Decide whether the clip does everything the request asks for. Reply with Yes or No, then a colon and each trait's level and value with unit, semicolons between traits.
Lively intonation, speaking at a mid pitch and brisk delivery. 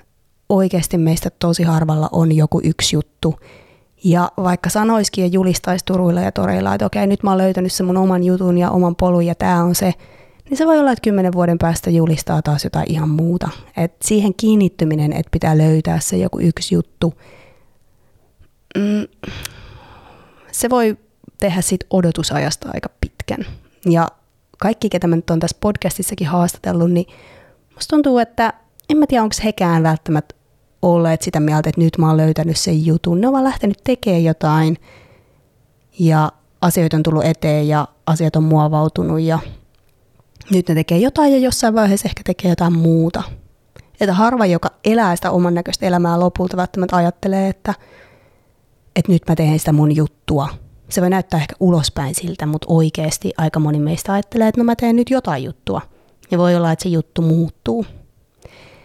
No: average, 3.3 semitones; medium, 170 Hz; fast, 170 wpm